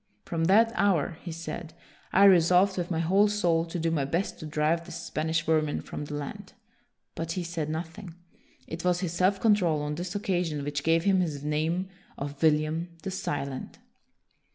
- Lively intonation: No, average, 3.0 semitones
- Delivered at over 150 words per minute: Yes, average, 185 wpm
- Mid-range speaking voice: Yes, medium, 165 Hz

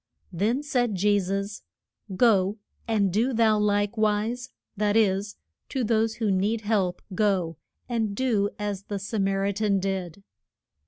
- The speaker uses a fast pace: No, average, 150 wpm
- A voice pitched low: No, high, 205 Hz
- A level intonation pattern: Yes, narrow, 2.1 semitones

